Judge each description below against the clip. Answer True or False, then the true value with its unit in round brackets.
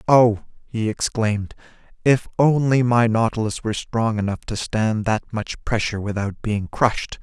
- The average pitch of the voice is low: True (110 Hz)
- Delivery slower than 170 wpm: True (150 wpm)